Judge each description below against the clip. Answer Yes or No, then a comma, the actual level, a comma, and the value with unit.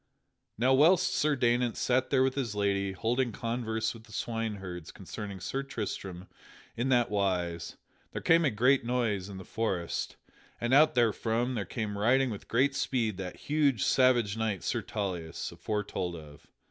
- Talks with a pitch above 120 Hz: No, low, 115 Hz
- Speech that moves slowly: No, average, 160 wpm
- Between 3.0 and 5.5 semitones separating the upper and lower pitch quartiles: Yes, average, 4.5 semitones